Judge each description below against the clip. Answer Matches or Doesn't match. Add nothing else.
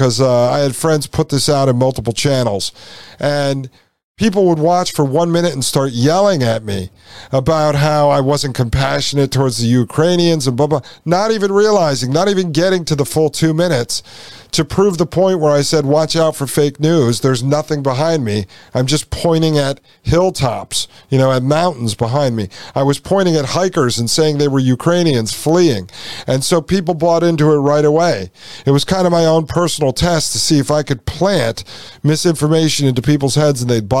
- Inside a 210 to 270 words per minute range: Doesn't match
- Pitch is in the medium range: Matches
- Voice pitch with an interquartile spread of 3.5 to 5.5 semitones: Matches